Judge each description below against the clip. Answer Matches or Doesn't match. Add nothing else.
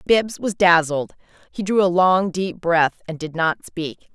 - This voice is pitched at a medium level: Matches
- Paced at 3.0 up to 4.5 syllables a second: Matches